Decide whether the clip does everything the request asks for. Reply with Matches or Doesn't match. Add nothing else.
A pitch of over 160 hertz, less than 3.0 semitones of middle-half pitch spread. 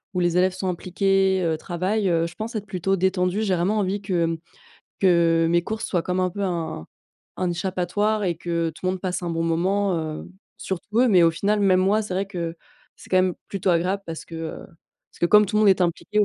Matches